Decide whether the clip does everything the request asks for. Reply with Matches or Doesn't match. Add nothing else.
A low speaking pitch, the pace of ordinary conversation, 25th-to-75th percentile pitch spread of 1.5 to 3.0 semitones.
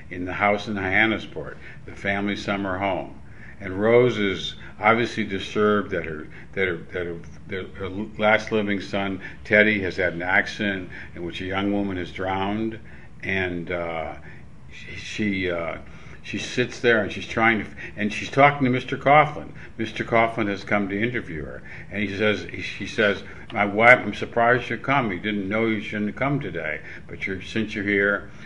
Matches